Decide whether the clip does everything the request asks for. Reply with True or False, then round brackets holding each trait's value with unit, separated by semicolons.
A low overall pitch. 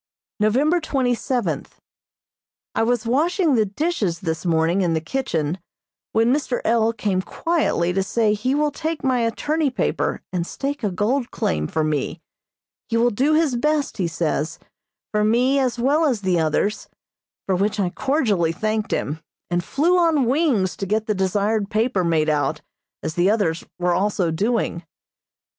False (215 Hz)